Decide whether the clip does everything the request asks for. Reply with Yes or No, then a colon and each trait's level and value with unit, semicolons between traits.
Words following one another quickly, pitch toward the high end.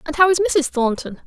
Yes: fast, 240 wpm; very high, 305 Hz